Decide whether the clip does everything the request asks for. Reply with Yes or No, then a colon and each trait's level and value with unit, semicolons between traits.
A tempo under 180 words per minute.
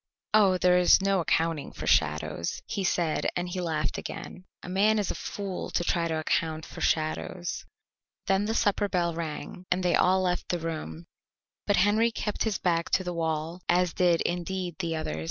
No: average, 190 wpm